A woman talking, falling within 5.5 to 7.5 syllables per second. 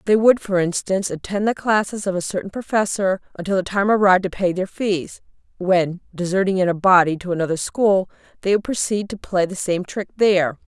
Yes: female; 5.6 syllables/s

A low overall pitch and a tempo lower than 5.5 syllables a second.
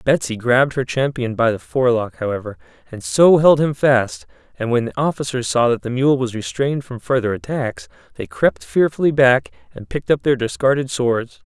Yes: low, 120 Hz; 5.3 syllables/s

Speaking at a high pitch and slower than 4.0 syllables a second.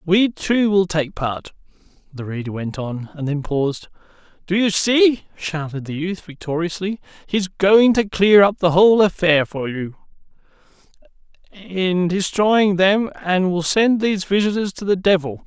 No: medium, 180 Hz; 3.0 syllables/s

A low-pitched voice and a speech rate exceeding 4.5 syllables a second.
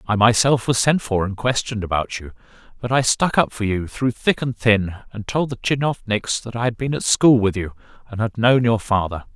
Yes: low, 115 Hz; 5.2 syllables/s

